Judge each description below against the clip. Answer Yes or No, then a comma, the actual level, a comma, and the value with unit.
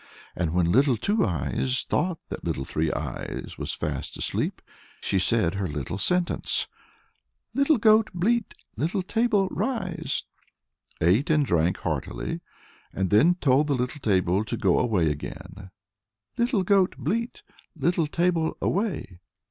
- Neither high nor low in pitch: Yes, medium, 145 Hz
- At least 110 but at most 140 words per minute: Yes, slow, 135 wpm